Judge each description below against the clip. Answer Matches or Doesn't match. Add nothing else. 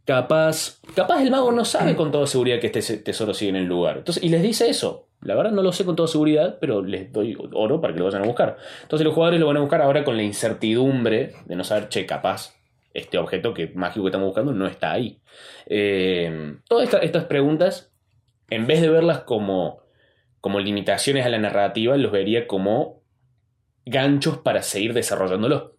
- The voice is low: Matches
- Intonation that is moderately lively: Doesn't match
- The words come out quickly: Matches